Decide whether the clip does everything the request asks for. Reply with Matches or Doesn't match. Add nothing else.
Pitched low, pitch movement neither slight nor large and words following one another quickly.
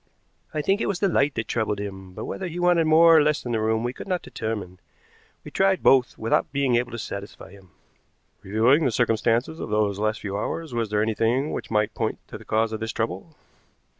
Doesn't match